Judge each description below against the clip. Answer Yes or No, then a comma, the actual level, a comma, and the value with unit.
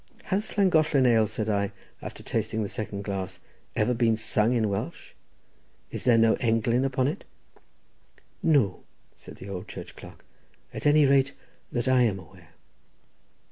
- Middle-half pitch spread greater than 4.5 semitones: No, average, 3.9 semitones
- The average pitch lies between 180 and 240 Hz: No, low, 115 Hz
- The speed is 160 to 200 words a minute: No, average, 150 wpm